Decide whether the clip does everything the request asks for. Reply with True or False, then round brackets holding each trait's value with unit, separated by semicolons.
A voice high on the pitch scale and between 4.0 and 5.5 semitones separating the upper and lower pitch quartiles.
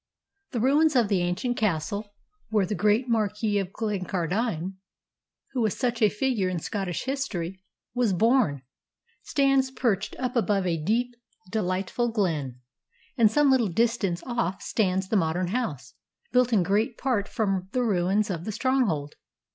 True (210 Hz; 4.7 semitones)